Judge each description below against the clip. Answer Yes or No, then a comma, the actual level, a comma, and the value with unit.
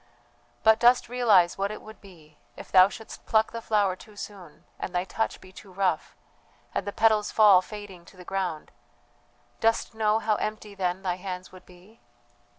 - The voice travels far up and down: No, average, 3.0 semitones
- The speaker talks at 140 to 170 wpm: No, average, 180 wpm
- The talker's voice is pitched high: Yes, high, 200 Hz